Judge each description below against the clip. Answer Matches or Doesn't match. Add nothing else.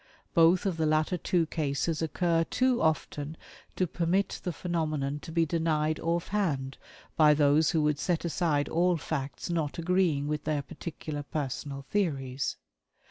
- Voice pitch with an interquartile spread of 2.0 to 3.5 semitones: Matches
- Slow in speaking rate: Doesn't match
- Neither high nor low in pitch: Matches